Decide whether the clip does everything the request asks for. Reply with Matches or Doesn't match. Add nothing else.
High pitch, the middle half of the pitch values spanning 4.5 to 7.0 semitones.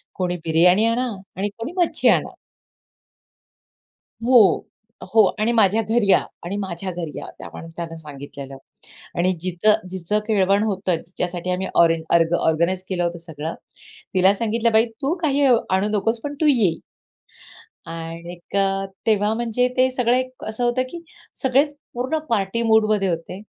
Matches